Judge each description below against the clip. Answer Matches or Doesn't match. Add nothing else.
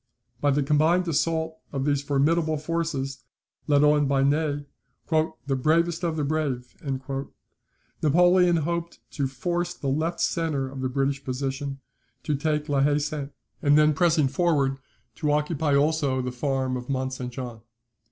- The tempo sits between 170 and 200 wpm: Doesn't match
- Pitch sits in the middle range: Matches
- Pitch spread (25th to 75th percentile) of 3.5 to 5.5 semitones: Doesn't match